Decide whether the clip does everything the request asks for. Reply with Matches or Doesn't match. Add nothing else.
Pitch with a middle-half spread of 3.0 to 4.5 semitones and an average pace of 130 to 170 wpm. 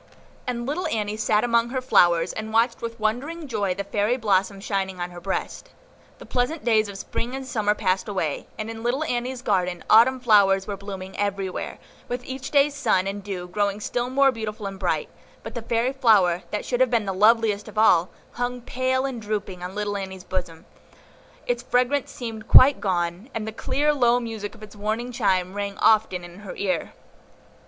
Doesn't match